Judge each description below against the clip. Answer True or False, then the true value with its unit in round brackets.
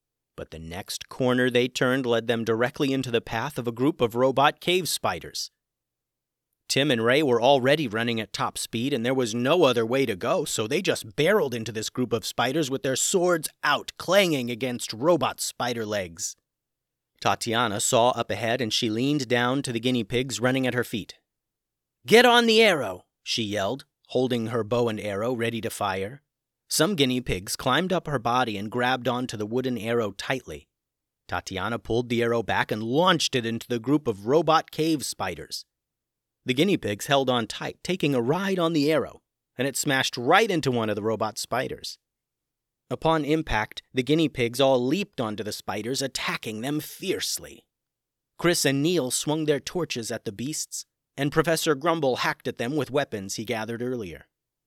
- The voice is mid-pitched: False (125 Hz)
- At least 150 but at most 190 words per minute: True (185 wpm)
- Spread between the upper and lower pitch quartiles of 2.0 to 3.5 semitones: False (4.1 semitones)